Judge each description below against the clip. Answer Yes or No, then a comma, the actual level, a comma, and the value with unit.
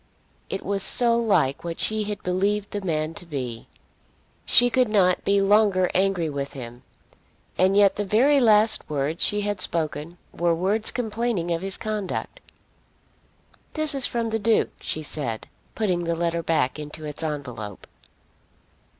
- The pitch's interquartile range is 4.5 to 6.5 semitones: Yes, average, 5.2 semitones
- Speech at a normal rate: Yes, average, 155 wpm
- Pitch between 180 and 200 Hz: Yes, high, 190 Hz